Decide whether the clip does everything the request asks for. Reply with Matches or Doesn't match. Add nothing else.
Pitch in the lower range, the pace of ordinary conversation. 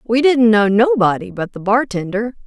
Doesn't match